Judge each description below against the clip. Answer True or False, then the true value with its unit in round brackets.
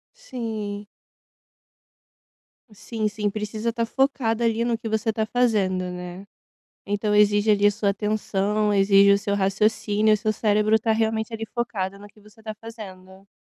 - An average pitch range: False (1.7 semitones)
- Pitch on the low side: False (210 Hz)